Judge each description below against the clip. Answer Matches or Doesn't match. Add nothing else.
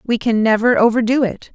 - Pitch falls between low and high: Doesn't match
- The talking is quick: Doesn't match